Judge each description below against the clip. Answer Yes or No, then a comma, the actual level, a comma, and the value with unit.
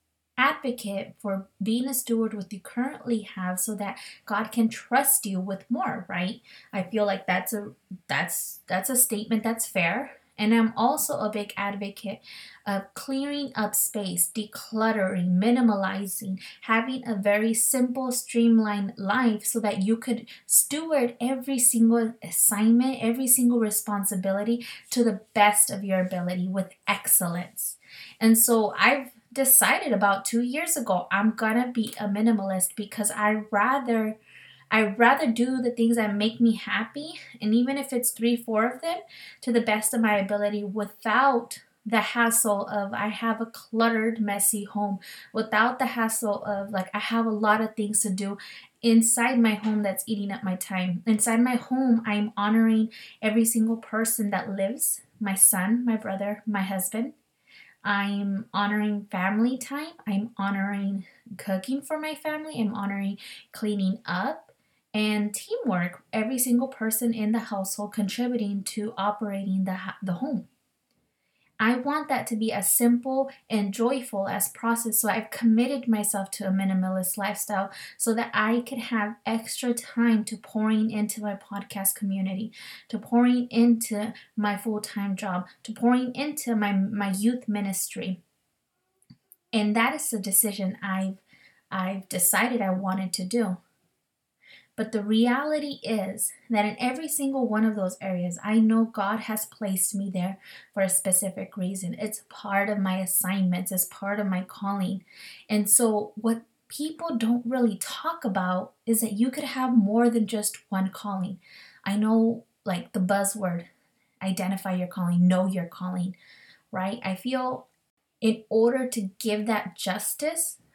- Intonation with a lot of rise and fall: No, average, 3.0 semitones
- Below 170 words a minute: Yes, average, 155 wpm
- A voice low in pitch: No, high, 215 Hz